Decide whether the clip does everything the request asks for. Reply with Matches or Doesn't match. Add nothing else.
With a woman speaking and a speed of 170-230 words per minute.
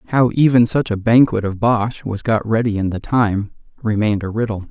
Doesn't match